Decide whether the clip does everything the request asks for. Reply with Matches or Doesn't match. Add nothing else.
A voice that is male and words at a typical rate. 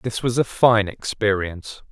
Matches